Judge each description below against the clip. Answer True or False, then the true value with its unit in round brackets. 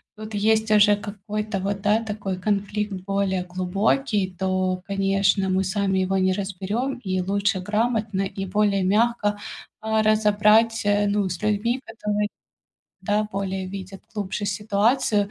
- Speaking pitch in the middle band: False (205 Hz)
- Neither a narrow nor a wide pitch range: False (1.8 semitones)